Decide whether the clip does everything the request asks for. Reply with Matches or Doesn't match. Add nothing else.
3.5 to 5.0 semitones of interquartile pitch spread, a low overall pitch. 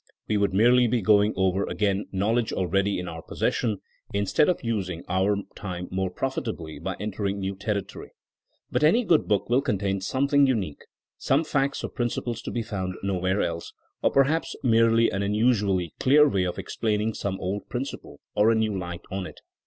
Matches